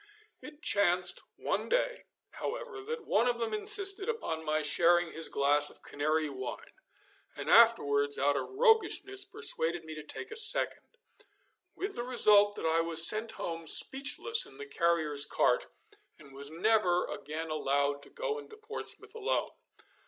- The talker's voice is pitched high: Yes, high, 200 Hz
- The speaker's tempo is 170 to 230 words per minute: No, average, 155 wpm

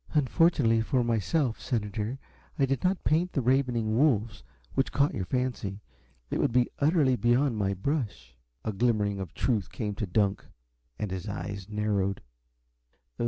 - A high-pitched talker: No, low, 115 Hz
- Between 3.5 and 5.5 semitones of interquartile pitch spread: Yes, average, 4.7 semitones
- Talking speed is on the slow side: No, average, 155 wpm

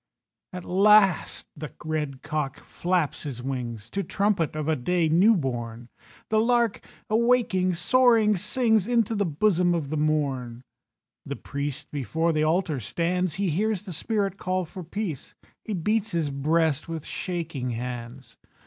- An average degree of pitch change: No, wide, 5.8 semitones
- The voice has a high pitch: No, medium, 170 Hz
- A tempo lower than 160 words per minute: Yes, average, 150 wpm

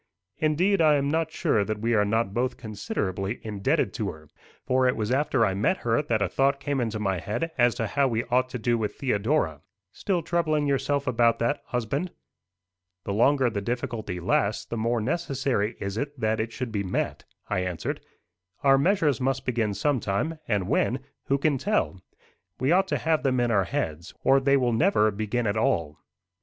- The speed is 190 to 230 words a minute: Yes, average, 195 wpm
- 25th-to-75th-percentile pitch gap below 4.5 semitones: No, average, 4.8 semitones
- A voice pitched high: No, low, 120 Hz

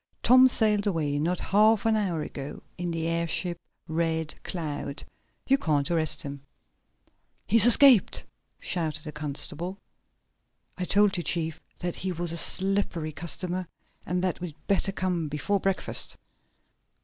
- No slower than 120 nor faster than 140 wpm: Yes, slow, 135 wpm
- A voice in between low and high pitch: Yes, medium, 175 Hz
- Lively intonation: No, average, 3.7 semitones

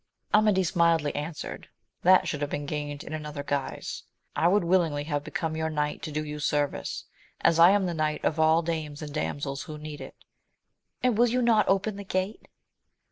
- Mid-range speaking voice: Yes, medium, 160 Hz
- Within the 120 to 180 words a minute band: No, average, 195 wpm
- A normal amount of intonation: Yes, average, 4.0 semitones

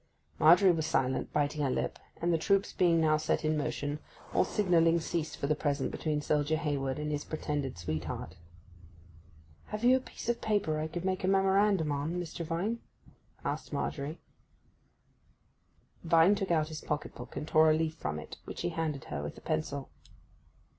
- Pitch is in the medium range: Yes, medium, 155 Hz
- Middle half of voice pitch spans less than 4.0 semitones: Yes, average, 3.0 semitones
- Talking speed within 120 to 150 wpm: No, average, 180 wpm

